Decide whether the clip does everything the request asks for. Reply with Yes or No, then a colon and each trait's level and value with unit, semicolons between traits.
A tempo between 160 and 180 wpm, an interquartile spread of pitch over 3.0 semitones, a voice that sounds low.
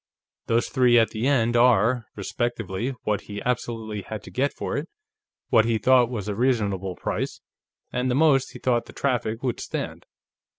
No: average, 175 wpm; average, 2.7 semitones; low, 120 Hz